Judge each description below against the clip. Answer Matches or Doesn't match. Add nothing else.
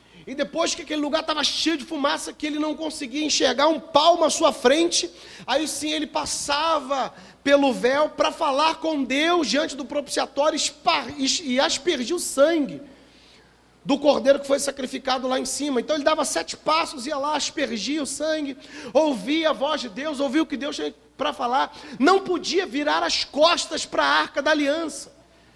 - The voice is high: Matches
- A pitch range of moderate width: Doesn't match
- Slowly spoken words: Doesn't match